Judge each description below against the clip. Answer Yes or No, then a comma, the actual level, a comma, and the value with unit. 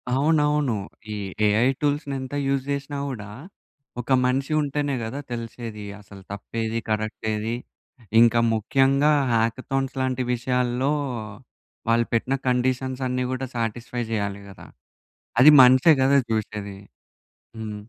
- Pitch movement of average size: Yes, average, 3.3 semitones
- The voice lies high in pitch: No, low, 125 Hz